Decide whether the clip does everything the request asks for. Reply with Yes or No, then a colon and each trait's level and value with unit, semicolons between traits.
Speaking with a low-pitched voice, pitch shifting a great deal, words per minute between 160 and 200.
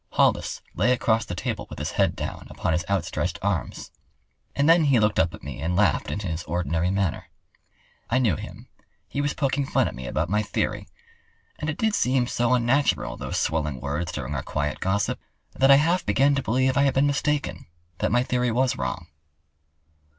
Yes: low, 110 Hz; wide, 8.2 semitones; average, 190 wpm